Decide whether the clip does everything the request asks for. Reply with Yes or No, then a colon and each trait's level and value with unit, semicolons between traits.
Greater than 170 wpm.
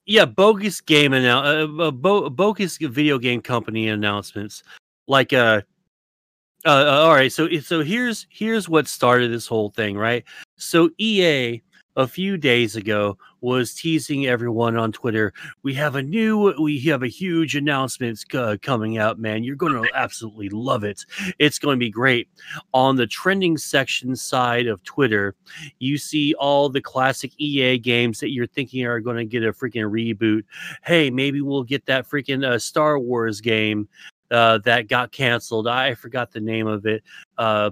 No: average, 165 wpm